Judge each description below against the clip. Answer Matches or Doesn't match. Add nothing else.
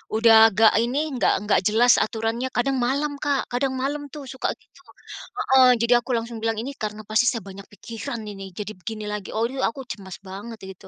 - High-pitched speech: Matches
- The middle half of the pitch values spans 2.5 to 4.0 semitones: Matches